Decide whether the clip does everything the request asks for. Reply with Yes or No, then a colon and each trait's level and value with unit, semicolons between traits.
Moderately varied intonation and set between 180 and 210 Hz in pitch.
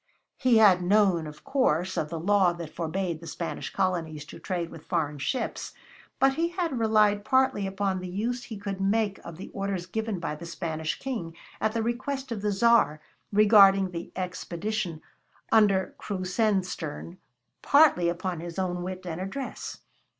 Yes: average, 4.2 semitones; high, 190 Hz